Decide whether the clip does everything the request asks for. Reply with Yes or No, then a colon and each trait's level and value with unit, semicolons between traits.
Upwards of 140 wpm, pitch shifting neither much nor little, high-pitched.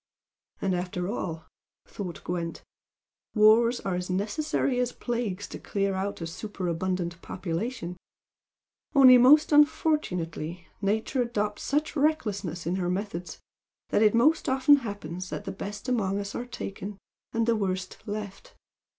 No: slow, 135 wpm; average, 4.9 semitones; high, 205 Hz